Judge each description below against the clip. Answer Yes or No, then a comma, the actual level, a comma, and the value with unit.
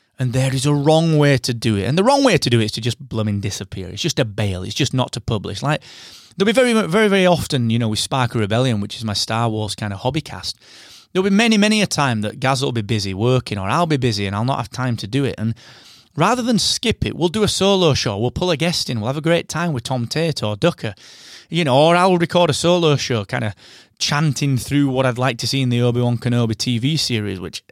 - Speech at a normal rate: No, fast, 270 wpm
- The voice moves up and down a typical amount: No, wide, 6.3 semitones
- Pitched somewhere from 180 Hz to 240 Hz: No, low, 130 Hz